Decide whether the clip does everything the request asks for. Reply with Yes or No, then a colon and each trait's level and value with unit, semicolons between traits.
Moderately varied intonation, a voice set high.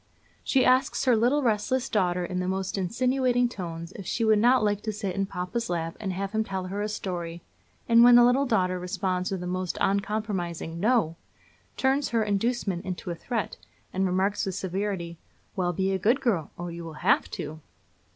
Yes: average, 4.3 semitones; high, 195 Hz